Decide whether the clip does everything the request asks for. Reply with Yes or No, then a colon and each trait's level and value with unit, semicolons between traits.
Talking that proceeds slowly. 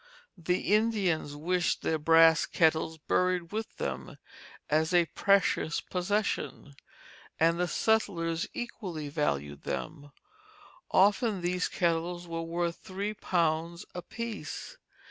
Yes: slow, 105 wpm